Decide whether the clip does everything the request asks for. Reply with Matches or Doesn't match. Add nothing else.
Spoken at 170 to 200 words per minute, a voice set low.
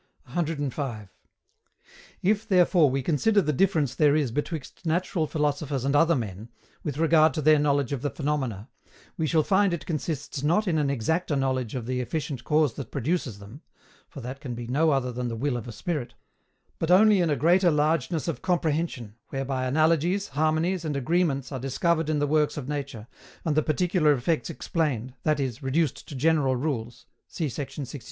Doesn't match